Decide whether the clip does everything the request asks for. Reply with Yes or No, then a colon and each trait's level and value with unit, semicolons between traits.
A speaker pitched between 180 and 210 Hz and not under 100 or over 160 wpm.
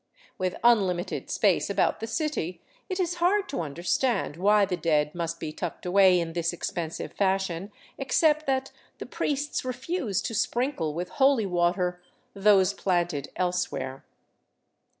Yes: high, 190 Hz; average, 145 wpm